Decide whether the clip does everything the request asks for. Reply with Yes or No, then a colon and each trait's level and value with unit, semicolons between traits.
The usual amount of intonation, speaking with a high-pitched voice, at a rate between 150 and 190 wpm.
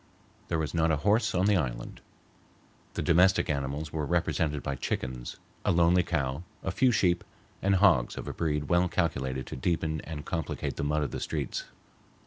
No: average, 3.8 semitones; very low, 80 Hz; average, 180 wpm